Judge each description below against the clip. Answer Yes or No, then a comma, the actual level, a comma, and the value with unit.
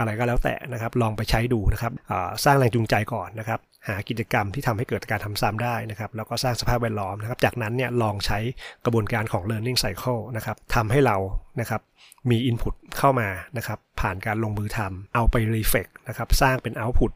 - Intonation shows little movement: Yes, narrow, 2.3 semitones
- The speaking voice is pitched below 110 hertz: No, low, 115 Hz